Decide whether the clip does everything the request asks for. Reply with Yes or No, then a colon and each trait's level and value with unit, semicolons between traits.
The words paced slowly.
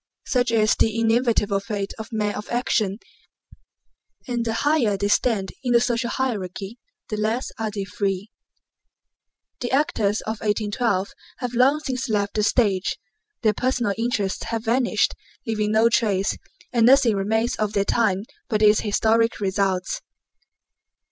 No: average, 145 wpm